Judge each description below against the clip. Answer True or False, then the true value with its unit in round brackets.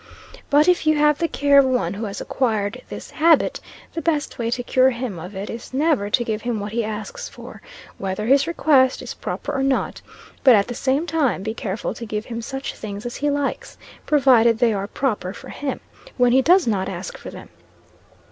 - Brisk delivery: True (215 wpm)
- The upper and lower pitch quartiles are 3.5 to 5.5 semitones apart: True (4.9 semitones)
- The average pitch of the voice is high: True (245 Hz)